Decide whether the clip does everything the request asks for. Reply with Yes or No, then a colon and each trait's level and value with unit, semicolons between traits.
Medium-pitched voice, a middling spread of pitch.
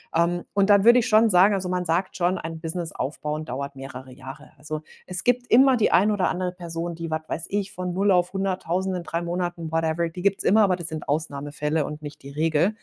Yes: medium, 175 Hz; average, 3.4 semitones